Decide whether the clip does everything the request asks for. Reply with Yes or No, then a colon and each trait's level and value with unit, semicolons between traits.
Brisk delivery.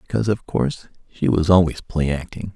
No: average, 190 wpm